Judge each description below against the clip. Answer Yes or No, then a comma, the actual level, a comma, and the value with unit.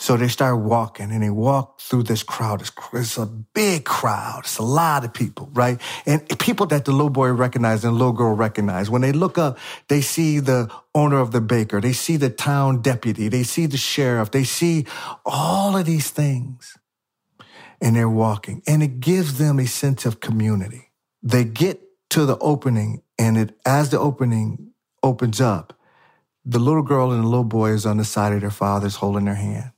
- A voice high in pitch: No, low, 125 Hz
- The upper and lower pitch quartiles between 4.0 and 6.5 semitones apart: Yes, average, 4.3 semitones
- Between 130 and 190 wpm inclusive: No, average, 200 wpm